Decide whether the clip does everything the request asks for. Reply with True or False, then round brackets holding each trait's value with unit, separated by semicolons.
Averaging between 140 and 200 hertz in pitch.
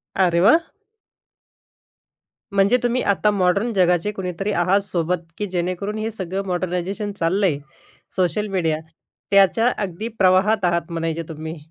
True (185 Hz)